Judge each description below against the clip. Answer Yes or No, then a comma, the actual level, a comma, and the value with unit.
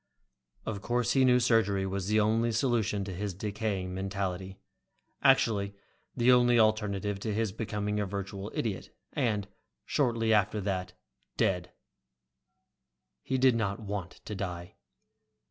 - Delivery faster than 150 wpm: No, slow, 135 wpm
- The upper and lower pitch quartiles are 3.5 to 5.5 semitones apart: No, average, 2.7 semitones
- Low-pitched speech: Yes, low, 105 Hz